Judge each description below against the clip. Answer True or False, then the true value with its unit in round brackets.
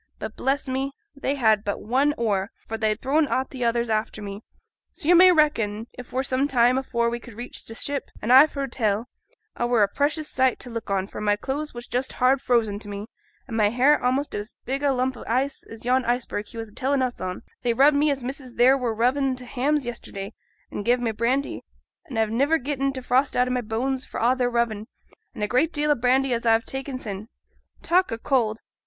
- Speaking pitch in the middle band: False (250 Hz)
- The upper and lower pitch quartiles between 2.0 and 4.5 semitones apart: True (3.2 semitones)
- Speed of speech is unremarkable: False (235 wpm)